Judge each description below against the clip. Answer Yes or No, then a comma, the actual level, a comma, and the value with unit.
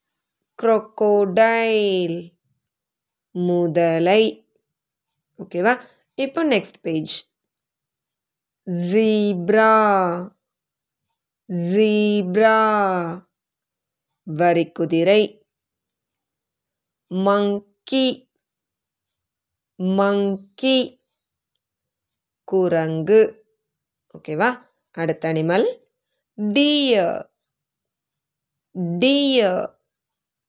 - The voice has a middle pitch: No, high, 200 Hz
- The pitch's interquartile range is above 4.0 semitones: Yes, average, 4.5 semitones